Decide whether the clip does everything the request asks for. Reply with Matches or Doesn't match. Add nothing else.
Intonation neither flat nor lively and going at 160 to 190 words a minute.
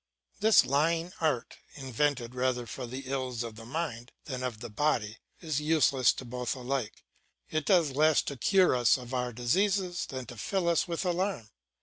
Matches